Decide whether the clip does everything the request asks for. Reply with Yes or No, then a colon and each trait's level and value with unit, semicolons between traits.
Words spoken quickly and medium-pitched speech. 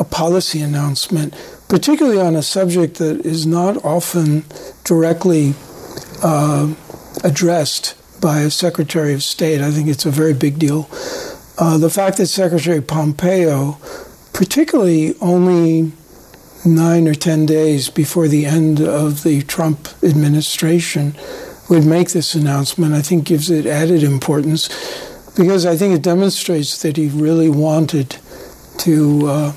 No: slow, 135 wpm; medium, 160 Hz